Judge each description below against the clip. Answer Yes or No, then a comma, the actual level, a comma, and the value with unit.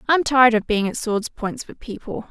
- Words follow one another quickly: Yes, fast, 235 wpm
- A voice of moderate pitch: No, high, 235 Hz